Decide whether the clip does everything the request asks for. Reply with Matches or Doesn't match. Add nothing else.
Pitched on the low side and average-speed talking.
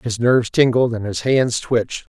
Matches